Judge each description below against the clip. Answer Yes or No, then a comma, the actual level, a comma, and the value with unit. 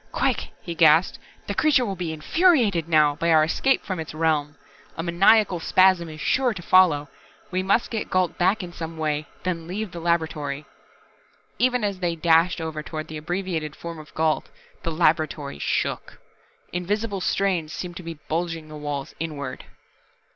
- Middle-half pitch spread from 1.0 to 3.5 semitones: Yes, average, 3.2 semitones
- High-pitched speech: No, medium, 170 Hz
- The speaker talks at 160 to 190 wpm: Yes, average, 170 wpm